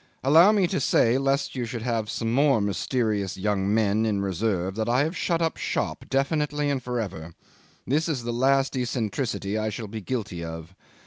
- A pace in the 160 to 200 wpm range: Yes, average, 190 wpm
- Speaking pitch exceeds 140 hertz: No, low, 115 Hz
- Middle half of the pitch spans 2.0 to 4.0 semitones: No, average, 4.9 semitones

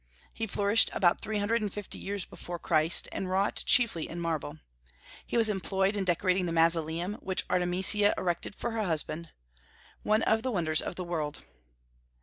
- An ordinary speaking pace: Yes, average, 170 wpm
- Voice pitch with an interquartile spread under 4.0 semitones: Yes, average, 3.6 semitones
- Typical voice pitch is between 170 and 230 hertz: Yes, medium, 185 Hz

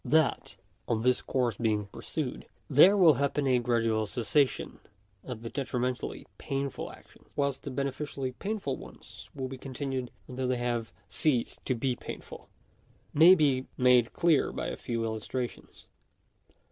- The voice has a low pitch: Yes, low, 130 Hz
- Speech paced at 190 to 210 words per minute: No, average, 145 wpm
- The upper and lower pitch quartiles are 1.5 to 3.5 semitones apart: Yes, average, 2.7 semitones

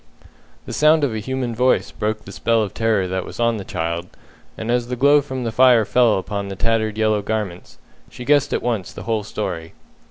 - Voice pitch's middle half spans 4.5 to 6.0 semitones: No, average, 3.4 semitones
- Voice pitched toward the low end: Yes, low, 110 Hz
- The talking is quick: Yes, fast, 215 wpm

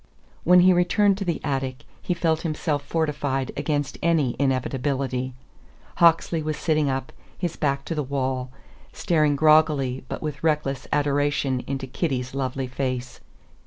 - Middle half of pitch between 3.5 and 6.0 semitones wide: No, average, 3.1 semitones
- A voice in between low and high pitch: Yes, medium, 145 Hz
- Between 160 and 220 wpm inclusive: No, average, 140 wpm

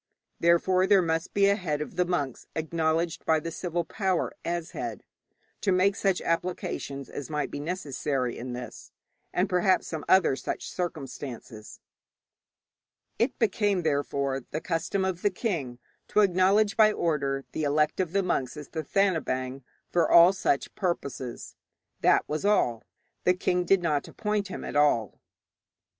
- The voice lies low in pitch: No, medium, 170 Hz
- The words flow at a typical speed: Yes, average, 150 wpm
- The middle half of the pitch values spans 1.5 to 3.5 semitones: No, average, 4.7 semitones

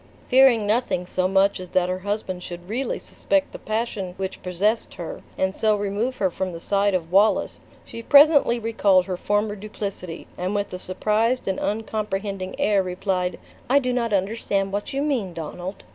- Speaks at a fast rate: No, average, 175 wpm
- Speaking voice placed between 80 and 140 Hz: No, high, 200 Hz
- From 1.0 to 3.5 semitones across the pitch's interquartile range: Yes, average, 3.1 semitones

